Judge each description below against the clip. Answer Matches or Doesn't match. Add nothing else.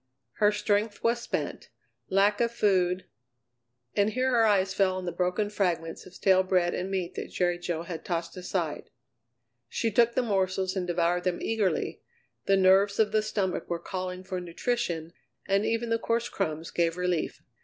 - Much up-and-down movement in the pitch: Doesn't match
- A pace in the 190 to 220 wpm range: Doesn't match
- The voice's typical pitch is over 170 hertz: Matches